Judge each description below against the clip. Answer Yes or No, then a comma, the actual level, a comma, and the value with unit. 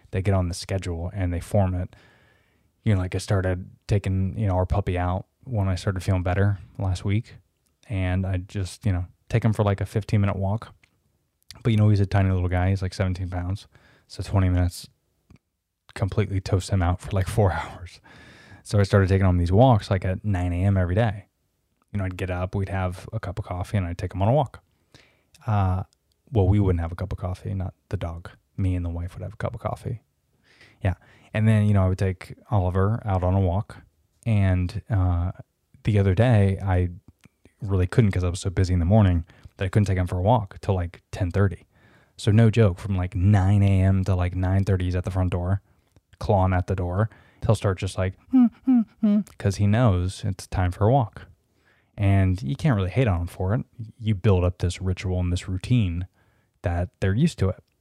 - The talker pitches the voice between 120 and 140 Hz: No, very low, 95 Hz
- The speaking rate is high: Yes, fast, 220 wpm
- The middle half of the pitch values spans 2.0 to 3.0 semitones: Yes, narrow, 2.4 semitones